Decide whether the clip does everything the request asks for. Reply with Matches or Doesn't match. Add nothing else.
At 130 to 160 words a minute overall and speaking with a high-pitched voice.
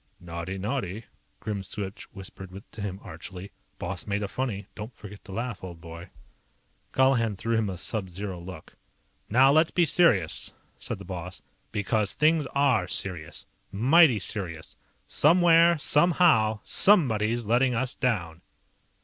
Doesn't match